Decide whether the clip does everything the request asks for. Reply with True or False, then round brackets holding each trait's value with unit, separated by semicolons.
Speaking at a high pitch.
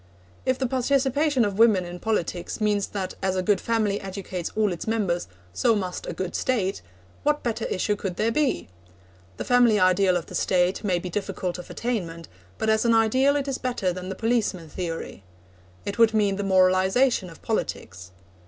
True (200 Hz)